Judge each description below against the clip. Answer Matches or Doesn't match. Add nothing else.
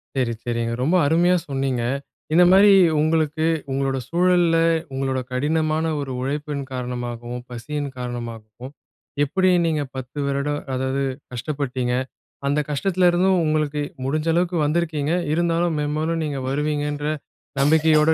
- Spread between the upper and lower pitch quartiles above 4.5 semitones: Doesn't match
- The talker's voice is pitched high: Doesn't match